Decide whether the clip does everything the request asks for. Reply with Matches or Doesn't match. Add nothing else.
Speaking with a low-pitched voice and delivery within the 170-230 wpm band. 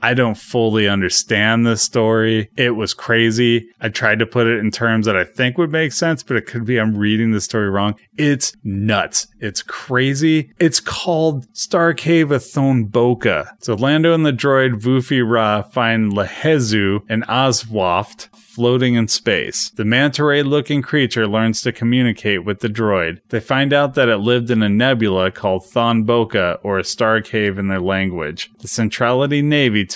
Matches